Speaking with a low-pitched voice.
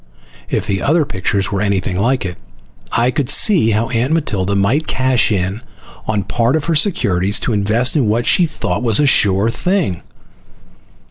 Yes: low, 110 Hz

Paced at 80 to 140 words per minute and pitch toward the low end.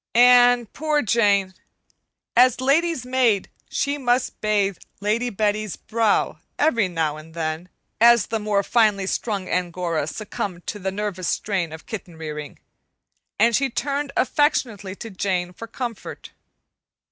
No: slow, 135 wpm; high, 210 Hz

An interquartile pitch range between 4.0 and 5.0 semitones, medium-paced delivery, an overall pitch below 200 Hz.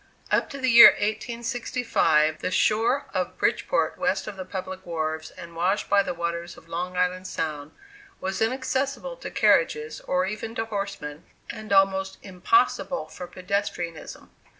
Yes: average, 4.7 semitones; average, 150 wpm; high, 190 Hz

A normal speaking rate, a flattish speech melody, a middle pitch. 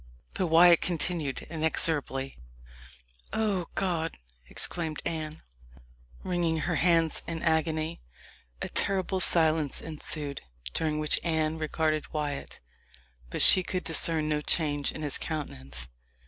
No: slow, 115 wpm; narrow, 1.9 semitones; medium, 160 Hz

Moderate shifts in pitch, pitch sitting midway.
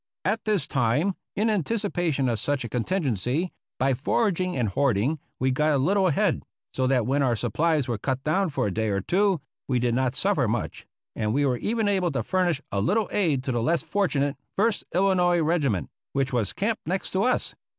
No: wide, 6.7 semitones; medium, 150 Hz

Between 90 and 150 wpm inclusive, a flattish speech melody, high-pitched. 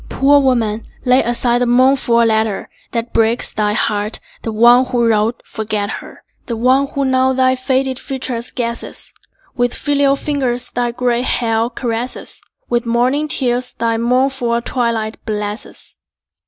Yes: average, 140 wpm; narrow, 2.2 semitones; high, 240 Hz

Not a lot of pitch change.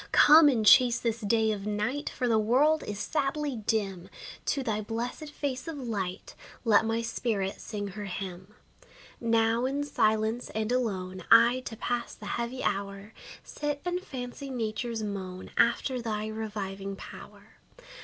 No: average, 3.4 semitones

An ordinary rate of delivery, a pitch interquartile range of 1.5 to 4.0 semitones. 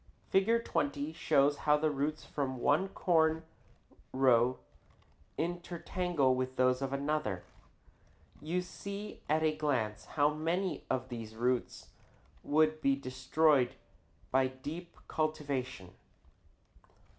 No: slow, 110 wpm; average, 3.6 semitones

